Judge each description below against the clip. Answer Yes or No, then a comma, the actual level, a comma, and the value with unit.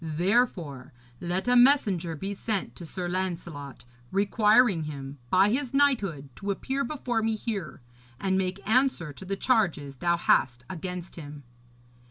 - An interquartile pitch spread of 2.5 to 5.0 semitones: No, wide, 5.5 semitones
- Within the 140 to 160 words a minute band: Yes, average, 145 wpm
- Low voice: No, high, 190 Hz